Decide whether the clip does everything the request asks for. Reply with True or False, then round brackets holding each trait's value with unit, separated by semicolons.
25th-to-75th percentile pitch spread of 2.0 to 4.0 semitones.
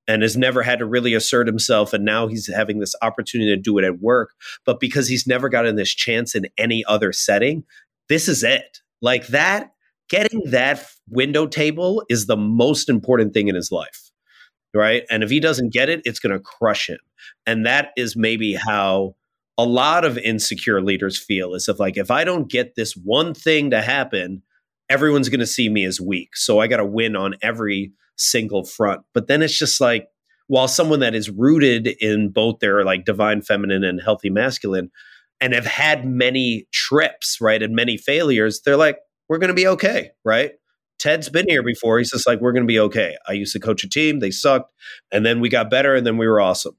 False (4.6 semitones)